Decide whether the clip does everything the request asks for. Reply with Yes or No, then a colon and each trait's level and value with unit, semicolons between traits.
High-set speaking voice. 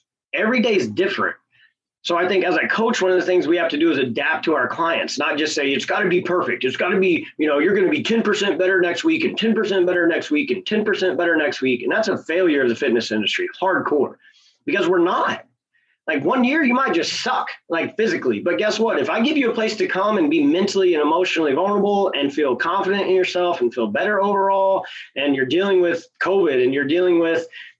Yes: high, 195 Hz